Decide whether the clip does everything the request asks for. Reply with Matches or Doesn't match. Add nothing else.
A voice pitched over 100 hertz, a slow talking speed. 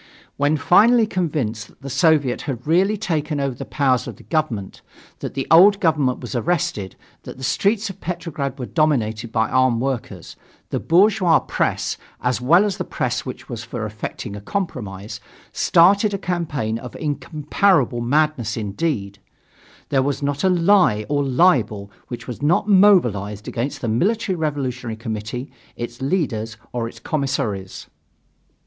Doesn't match